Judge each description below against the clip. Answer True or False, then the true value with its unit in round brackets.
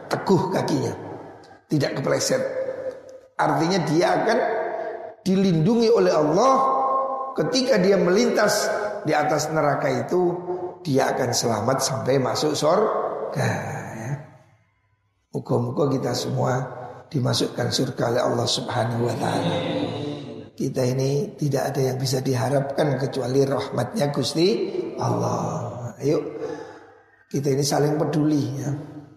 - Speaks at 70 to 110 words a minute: True (105 wpm)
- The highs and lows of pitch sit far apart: True (8.9 semitones)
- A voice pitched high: False (150 Hz)